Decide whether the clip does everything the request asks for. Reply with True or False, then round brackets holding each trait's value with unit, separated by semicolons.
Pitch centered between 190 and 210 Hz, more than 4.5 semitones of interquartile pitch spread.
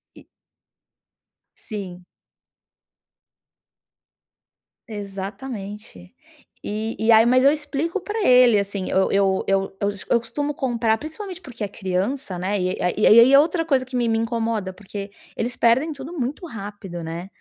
False (225 Hz; 5.2 semitones)